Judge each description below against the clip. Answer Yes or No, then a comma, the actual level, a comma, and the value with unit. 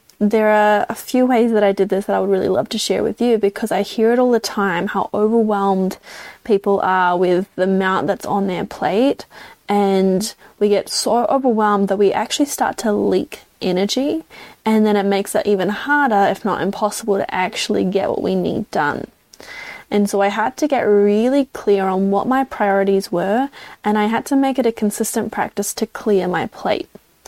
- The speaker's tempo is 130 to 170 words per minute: No, average, 200 wpm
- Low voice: No, high, 205 Hz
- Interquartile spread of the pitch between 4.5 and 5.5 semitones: No, narrow, 2.5 semitones